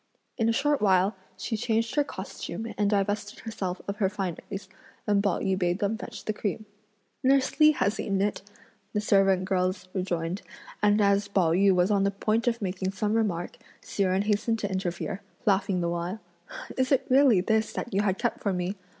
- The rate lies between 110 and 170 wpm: No, average, 195 wpm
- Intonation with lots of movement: No, average, 2.8 semitones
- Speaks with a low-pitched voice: No, high, 200 Hz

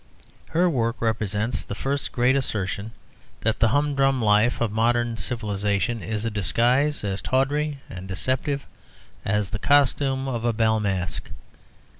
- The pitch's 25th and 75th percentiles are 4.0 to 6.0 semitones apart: Yes, average, 4.4 semitones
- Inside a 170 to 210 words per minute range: No, average, 140 wpm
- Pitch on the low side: Yes, low, 115 Hz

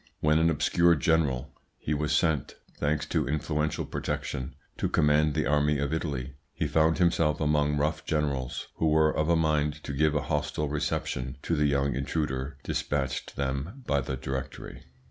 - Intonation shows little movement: Yes, narrow, 1.9 semitones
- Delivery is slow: No, average, 165 wpm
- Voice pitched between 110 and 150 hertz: No, very low, 75 Hz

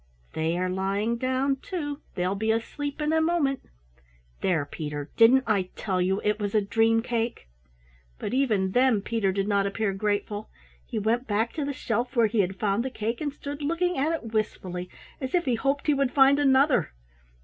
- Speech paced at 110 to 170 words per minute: No, average, 195 wpm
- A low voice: No, high, 225 Hz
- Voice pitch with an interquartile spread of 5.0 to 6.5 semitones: Yes, wide, 5.6 semitones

